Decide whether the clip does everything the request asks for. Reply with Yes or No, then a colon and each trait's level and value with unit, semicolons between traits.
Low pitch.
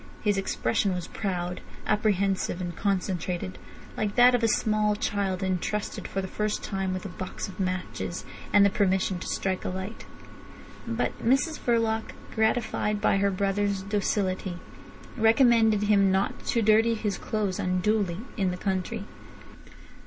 No: high, 200 Hz